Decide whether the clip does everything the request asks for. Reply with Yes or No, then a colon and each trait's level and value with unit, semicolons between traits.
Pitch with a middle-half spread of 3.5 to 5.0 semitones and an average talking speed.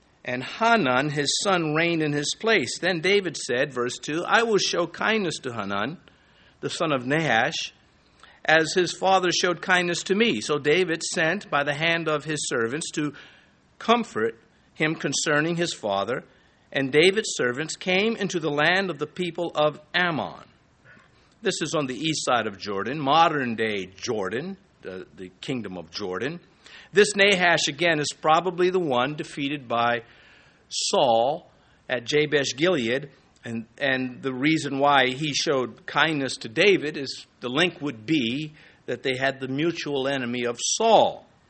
Yes: average, 4.7 semitones; average, 160 wpm